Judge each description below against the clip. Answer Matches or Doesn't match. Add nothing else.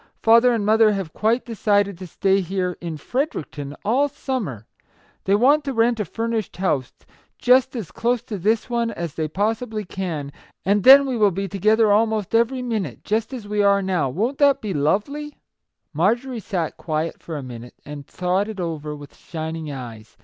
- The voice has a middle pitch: Doesn't match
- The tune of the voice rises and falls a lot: Matches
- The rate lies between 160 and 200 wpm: Matches